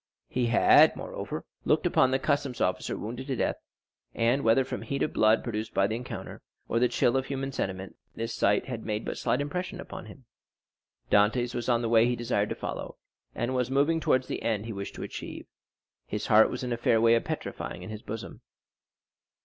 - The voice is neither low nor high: No, low, 120 Hz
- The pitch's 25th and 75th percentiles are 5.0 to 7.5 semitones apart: No, average, 2.9 semitones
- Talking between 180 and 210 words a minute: Yes, fast, 205 wpm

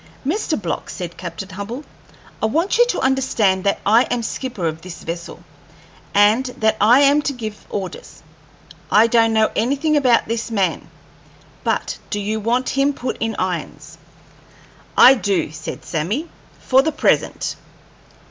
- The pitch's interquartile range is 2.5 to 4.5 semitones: No, average, 4.9 semitones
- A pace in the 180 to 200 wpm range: No, average, 150 wpm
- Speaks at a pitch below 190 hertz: No, high, 225 Hz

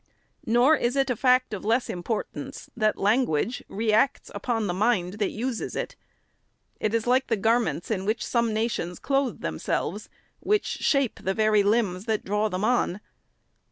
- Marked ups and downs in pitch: No, average, 3.0 semitones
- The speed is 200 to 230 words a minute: No, average, 165 wpm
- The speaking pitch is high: Yes, high, 220 Hz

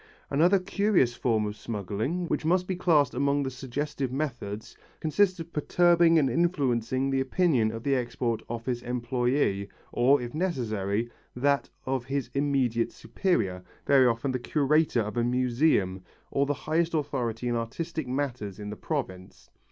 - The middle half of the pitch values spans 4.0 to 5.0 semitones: Yes, average, 4.6 semitones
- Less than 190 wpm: Yes, average, 150 wpm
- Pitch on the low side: Yes, low, 130 Hz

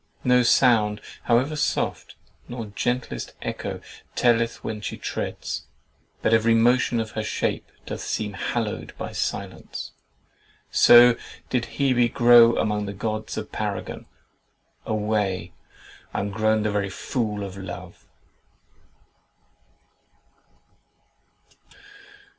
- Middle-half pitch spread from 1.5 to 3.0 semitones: Yes, narrow, 2.4 semitones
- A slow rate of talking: Yes, slow, 105 wpm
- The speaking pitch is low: Yes, low, 110 Hz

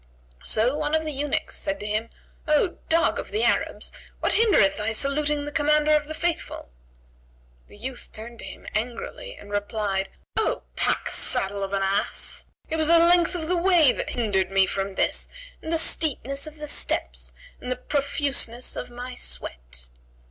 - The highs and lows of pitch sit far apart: Yes, wide, 6.8 semitones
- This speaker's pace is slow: No, average, 175 wpm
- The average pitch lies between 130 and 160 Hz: No, very high, 275 Hz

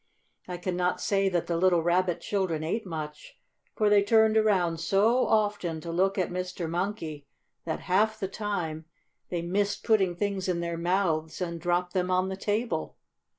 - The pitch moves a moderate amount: Yes, average, 3.0 semitones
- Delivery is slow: No, average, 175 wpm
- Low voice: No, medium, 180 Hz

